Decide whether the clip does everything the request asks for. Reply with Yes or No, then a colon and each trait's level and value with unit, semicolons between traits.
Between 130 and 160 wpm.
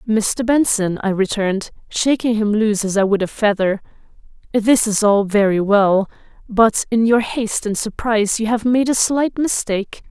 No: average, 170 wpm